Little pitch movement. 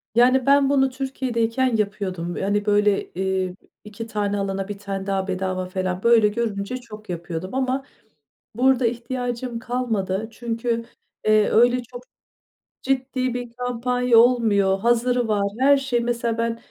No: average, 3.8 semitones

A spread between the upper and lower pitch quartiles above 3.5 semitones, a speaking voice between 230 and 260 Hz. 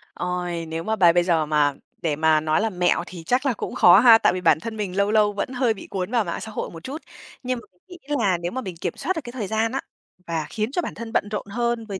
No: average, 5.2 semitones; high, 200 Hz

